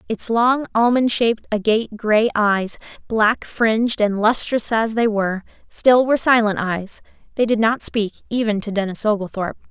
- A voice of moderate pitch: No, high, 220 Hz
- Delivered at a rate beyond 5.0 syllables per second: No, 4.9 syllables/s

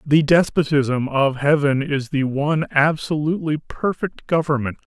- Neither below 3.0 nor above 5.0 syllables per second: Yes, 4.6 syllables/s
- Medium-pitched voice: Yes, medium, 145 Hz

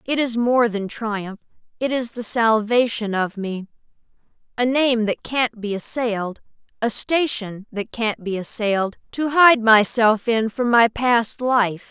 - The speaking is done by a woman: Yes, female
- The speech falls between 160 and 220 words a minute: No, average, 150 wpm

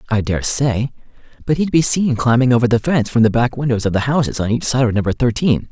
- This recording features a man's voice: Yes, male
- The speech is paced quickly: Yes, fast, 240 wpm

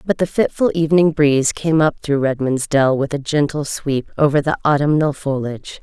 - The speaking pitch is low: No, medium, 145 Hz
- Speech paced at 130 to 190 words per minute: Yes, average, 185 wpm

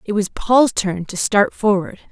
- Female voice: Yes, female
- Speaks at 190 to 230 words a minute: Yes, average, 200 wpm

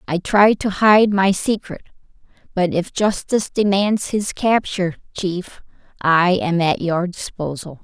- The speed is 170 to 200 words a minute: No, average, 140 wpm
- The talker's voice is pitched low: No, high, 190 Hz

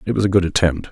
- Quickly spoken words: Yes, fast, 330 wpm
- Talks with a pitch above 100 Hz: No, very low, 90 Hz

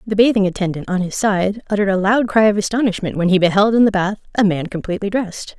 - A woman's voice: Yes, female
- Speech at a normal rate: No, fast, 235 wpm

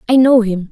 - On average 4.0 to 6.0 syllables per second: Yes, 5.7 syllables/s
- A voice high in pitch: Yes, high, 225 Hz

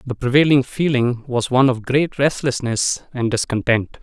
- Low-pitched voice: Yes, low, 130 Hz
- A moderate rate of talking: Yes, average, 150 wpm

